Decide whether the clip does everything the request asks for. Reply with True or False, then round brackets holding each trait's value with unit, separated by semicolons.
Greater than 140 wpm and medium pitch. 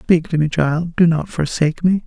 True (205 wpm; 165 Hz)